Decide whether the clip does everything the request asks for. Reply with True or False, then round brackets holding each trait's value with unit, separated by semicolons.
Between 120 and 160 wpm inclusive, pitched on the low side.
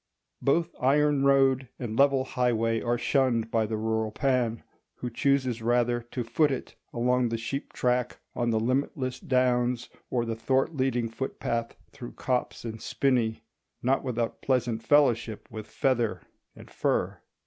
True (150 wpm; 125 Hz)